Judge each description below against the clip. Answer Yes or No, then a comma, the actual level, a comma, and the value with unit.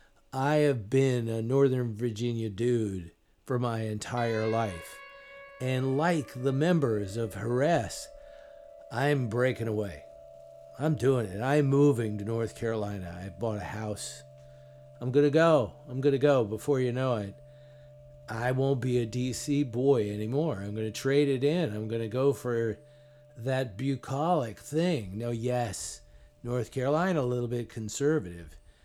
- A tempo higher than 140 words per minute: Yes, average, 150 wpm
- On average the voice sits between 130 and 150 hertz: No, low, 120 Hz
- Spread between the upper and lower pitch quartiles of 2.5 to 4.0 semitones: No, average, 4.9 semitones